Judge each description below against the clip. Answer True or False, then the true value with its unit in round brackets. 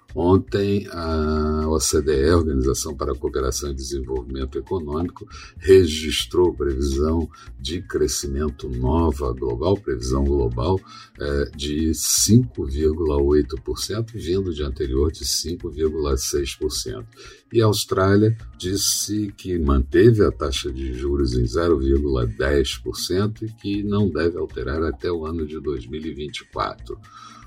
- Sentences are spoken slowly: True (105 wpm)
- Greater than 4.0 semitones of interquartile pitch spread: True (5.2 semitones)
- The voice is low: True (80 Hz)